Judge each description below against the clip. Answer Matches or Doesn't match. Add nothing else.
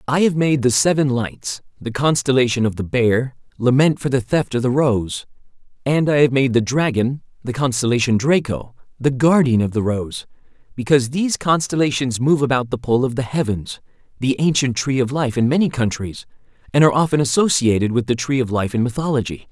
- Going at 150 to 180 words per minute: Doesn't match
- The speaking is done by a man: Matches